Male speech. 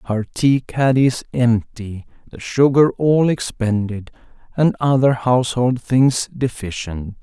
Yes: male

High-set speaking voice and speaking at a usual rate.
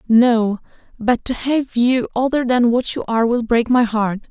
Yes: high, 235 Hz; average, 195 wpm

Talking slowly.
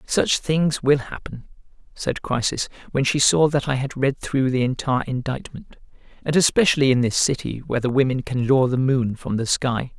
No: average, 190 wpm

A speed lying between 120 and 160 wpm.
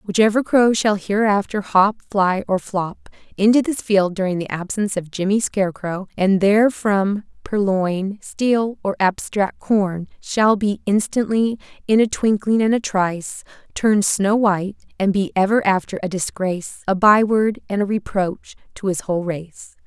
Yes: average, 155 wpm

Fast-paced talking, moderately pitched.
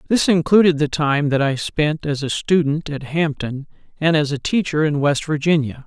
No: average, 195 wpm; medium, 150 Hz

